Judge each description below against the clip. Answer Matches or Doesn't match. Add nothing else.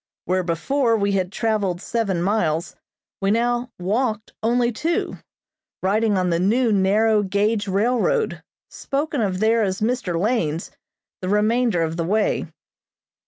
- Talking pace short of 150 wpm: Matches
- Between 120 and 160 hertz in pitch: Doesn't match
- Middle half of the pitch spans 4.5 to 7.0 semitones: Doesn't match